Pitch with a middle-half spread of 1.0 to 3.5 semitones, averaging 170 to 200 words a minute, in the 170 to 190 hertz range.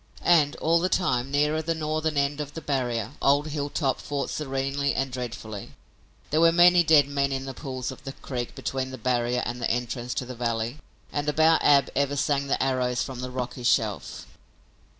No: average, 3.0 semitones; average, 190 wpm; low, 135 Hz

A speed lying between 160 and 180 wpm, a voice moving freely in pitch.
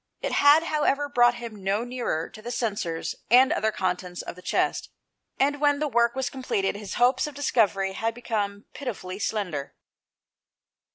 No: average, 165 wpm; average, 5.0 semitones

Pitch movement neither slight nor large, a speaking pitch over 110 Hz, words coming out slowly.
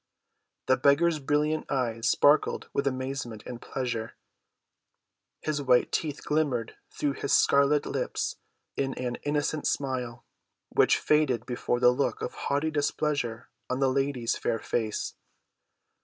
Yes: average, 3.1 semitones; low, 135 Hz; slow, 125 wpm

